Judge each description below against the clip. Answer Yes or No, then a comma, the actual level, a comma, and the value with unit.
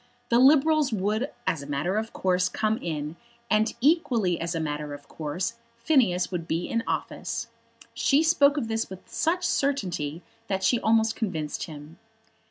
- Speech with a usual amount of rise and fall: No, wide, 6.7 semitones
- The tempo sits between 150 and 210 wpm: Yes, average, 165 wpm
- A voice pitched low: No, high, 200 Hz